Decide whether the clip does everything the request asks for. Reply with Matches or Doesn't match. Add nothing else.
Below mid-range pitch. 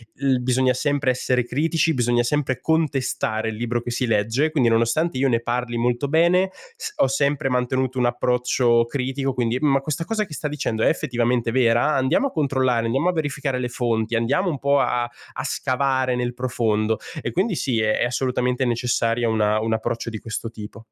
Matches